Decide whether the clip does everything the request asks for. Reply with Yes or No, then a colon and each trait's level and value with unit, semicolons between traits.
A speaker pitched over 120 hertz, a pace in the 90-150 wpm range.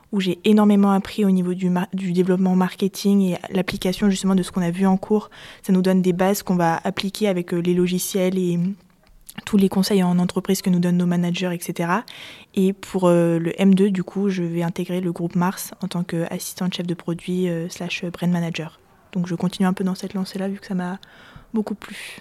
No: medium, 185 Hz; fast, 220 wpm